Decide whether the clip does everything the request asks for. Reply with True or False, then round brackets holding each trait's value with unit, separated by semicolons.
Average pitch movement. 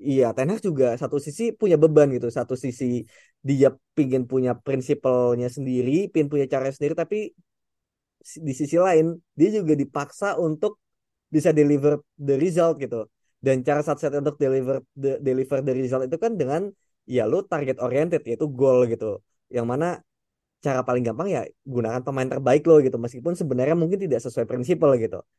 True (3.7 semitones)